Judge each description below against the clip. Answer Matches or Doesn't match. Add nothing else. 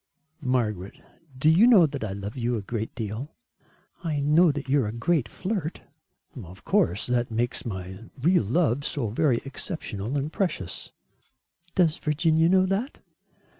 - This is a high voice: Doesn't match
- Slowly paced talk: Doesn't match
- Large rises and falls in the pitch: Matches